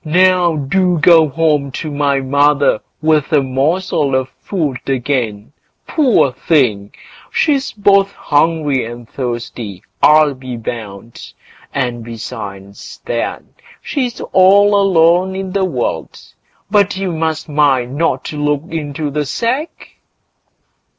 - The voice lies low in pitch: No, medium, 150 Hz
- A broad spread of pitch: Yes, wide, 5.7 semitones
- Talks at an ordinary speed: No, slow, 120 wpm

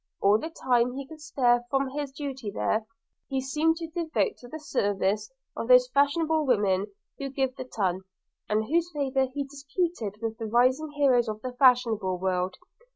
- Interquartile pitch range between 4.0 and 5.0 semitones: Yes, average, 4.7 semitones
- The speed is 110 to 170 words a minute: No, average, 180 wpm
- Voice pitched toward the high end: Yes, very high, 255 Hz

